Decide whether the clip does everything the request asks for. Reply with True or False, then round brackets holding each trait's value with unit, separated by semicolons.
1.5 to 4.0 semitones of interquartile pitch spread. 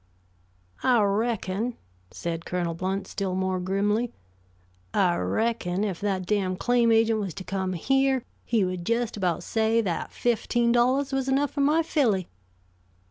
False (4.4 semitones)